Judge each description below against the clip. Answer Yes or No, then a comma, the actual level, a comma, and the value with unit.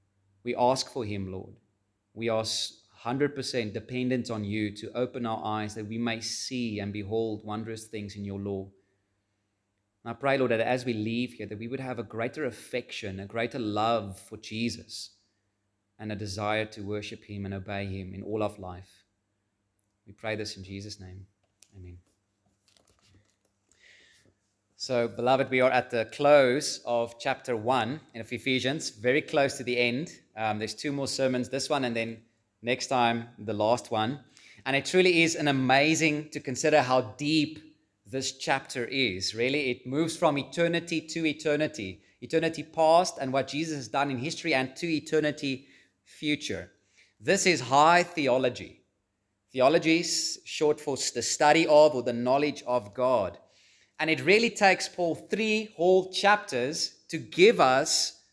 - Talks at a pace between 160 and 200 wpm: Yes, average, 165 wpm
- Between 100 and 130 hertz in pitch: Yes, low, 120 Hz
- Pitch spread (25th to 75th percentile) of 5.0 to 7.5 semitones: Yes, average, 5.3 semitones